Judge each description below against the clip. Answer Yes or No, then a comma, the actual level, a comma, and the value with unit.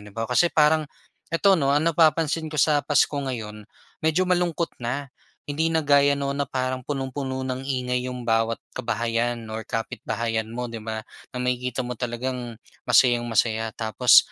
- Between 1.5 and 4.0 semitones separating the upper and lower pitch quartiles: Yes, average, 3.7 semitones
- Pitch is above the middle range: No, low, 130 Hz